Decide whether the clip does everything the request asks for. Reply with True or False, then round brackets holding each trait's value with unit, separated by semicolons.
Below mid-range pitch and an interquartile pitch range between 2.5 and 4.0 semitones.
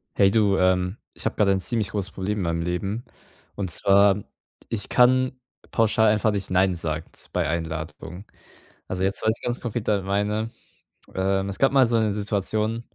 True (100 Hz; 2.9 semitones)